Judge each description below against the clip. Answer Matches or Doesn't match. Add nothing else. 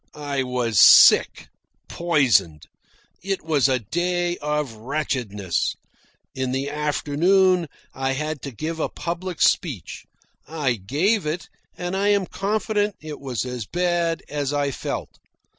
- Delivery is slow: Matches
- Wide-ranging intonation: Doesn't match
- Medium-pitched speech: Matches